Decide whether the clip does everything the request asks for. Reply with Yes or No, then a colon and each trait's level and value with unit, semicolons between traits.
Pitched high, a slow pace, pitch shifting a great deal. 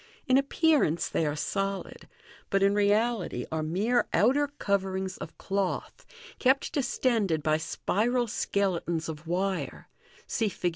Yes: high, 195 Hz; slow, 130 wpm; wide, 5.7 semitones